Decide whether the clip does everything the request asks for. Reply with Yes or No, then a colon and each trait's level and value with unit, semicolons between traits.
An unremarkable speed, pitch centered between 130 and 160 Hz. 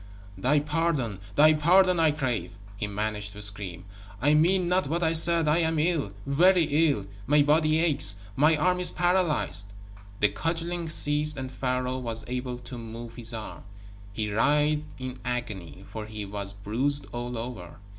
Yes: average, 165 wpm; low, 135 Hz